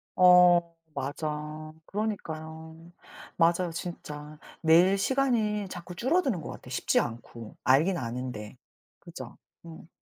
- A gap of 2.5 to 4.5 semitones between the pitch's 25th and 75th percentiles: Yes, average, 3.6 semitones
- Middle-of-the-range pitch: Yes, medium, 165 Hz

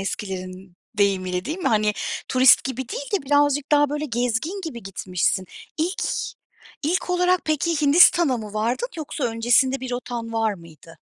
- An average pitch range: No, wide, 6.5 semitones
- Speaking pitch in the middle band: No, very high, 250 Hz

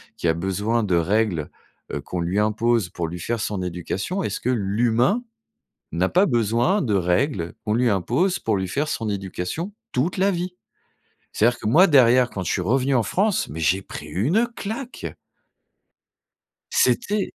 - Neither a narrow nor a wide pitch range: No, wide, 8.4 semitones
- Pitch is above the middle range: No, low, 115 Hz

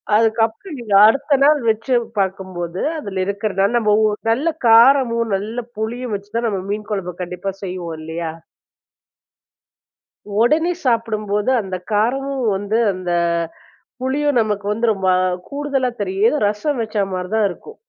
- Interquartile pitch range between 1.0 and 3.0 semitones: No, average, 4.2 semitones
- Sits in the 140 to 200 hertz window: No, high, 215 Hz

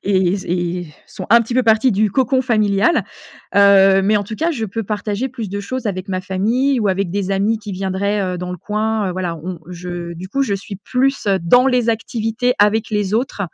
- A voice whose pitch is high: Yes, high, 205 Hz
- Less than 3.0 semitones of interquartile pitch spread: No, average, 3.3 semitones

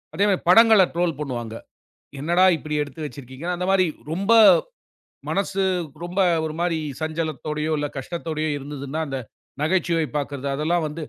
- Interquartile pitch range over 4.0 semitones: No, average, 3.3 semitones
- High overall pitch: No, medium, 155 Hz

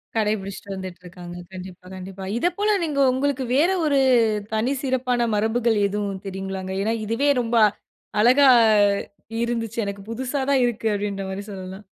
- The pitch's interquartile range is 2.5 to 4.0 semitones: No, average, 4.6 semitones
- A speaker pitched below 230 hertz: Yes, high, 215 Hz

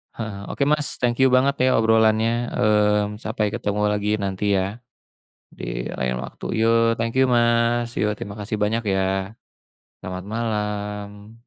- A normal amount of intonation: No, narrow, 2.3 semitones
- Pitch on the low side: Yes, low, 105 Hz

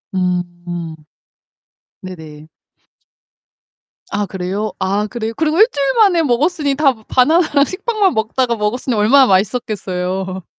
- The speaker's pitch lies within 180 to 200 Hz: No, high, 220 Hz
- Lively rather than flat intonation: Yes, wide, 7.2 semitones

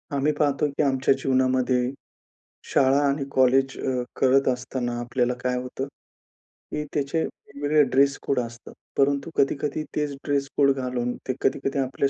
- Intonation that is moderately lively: No, narrow, 1.6 semitones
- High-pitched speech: No, low, 135 Hz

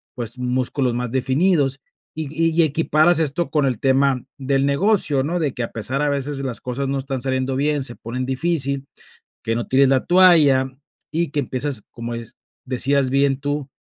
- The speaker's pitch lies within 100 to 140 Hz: Yes, low, 135 Hz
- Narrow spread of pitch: Yes, narrow, 2.3 semitones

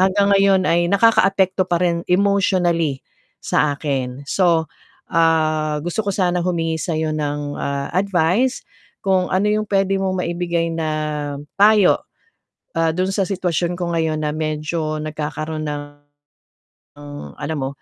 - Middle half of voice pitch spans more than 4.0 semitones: No, average, 3.6 semitones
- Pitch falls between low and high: Yes, medium, 170 Hz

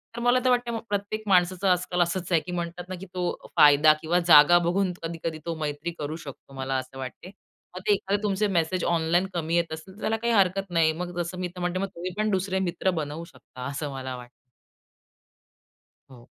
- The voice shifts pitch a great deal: No, average, 3.2 semitones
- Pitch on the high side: No, medium, 175 Hz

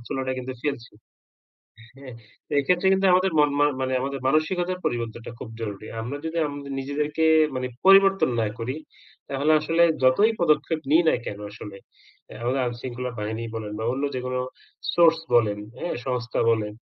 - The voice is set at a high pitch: No, low, 135 Hz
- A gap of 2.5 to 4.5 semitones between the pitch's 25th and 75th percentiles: No, average, 4.9 semitones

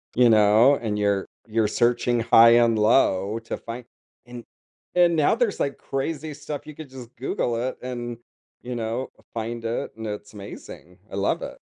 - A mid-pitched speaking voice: No, low, 120 Hz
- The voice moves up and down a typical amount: Yes, average, 3.0 semitones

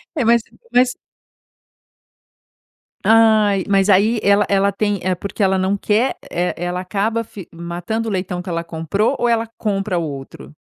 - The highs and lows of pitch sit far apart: No, average, 3.5 semitones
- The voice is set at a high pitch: Yes, high, 200 Hz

